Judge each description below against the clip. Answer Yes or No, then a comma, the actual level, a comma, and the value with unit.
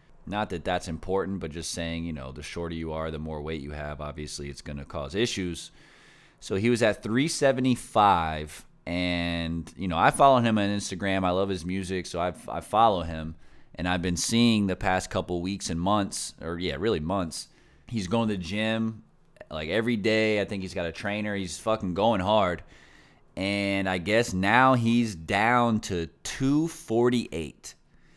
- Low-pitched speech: Yes, very low, 95 Hz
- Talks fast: No, average, 185 wpm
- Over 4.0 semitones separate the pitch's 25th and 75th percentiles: Yes, average, 4.7 semitones